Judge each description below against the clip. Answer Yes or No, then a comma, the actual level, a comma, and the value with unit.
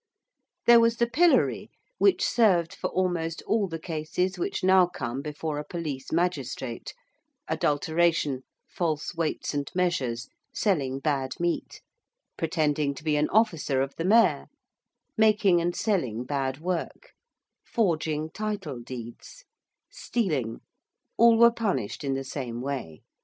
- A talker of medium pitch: Yes, medium, 160 Hz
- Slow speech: Yes, slow, 130 wpm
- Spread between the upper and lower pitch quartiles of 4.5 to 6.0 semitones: Yes, wide, 5.4 semitones